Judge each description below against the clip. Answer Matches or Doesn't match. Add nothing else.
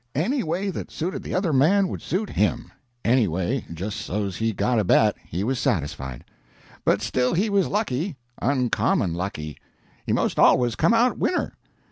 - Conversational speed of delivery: Matches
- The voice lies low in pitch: Matches